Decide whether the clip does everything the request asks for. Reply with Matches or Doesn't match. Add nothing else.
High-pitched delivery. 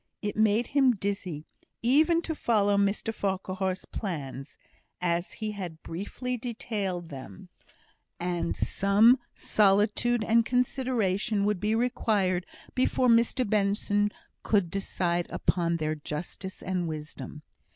Matches